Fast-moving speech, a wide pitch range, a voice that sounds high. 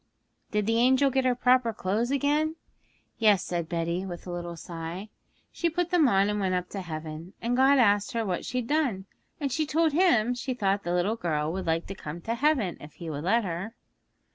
Yes: fast, 215 wpm; wide, 6.6 semitones; high, 210 Hz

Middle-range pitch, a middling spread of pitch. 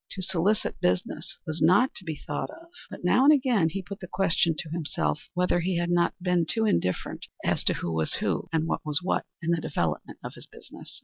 Yes: medium, 175 Hz; average, 3.6 semitones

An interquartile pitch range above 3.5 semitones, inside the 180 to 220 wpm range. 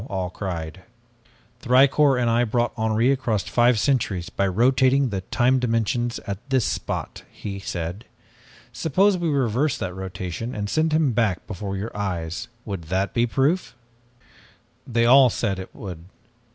No: average, 5.2 semitones; average, 150 wpm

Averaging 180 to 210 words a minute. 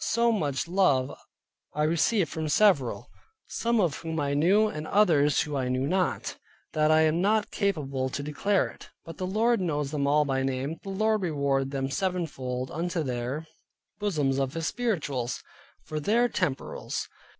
No: average, 160 wpm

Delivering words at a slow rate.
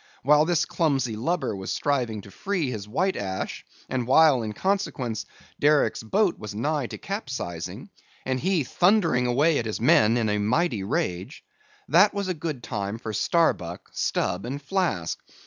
No: average, 160 wpm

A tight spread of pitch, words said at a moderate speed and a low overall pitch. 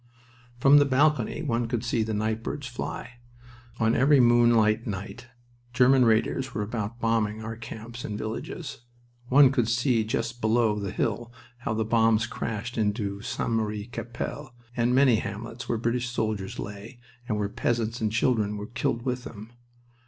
Yes: narrow, 2.1 semitones; average, 160 wpm; low, 115 Hz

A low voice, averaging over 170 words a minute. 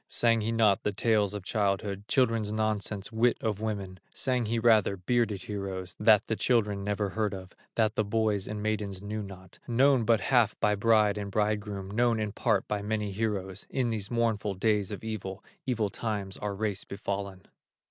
Yes: low, 105 Hz; average, 180 wpm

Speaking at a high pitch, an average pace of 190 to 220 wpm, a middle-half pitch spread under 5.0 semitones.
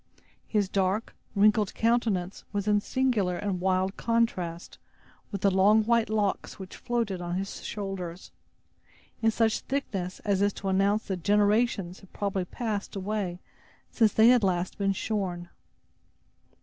No: high, 200 Hz; slow, 135 wpm; narrow, 2.6 semitones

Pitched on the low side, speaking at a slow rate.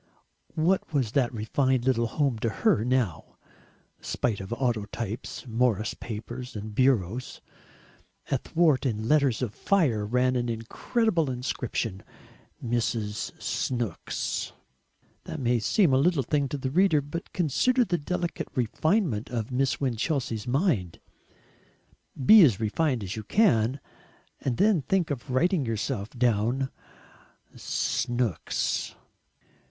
Yes: low, 125 Hz; slow, 120 wpm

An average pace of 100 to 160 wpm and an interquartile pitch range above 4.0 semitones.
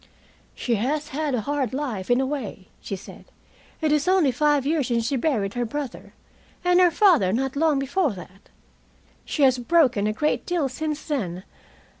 No: average, 180 wpm; average, 4.5 semitones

